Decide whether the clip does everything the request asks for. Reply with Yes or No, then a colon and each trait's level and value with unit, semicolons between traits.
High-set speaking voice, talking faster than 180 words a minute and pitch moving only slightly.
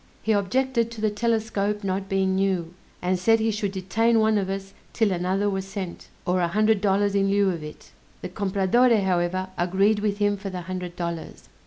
Yes: high, 195 Hz; average, 195 wpm; narrow, 2.3 semitones